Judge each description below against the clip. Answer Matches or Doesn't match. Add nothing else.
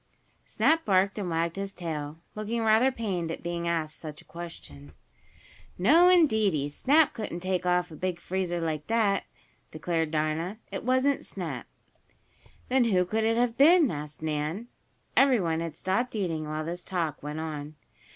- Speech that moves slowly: Doesn't match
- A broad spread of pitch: Matches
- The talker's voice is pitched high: Doesn't match